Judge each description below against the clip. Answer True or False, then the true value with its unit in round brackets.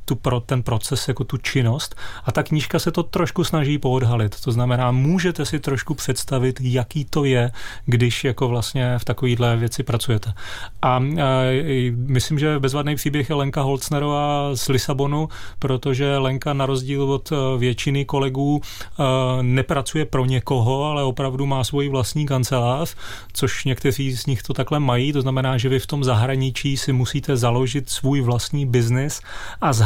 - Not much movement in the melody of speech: True (2.3 semitones)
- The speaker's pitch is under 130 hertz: False (135 Hz)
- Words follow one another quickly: False (160 wpm)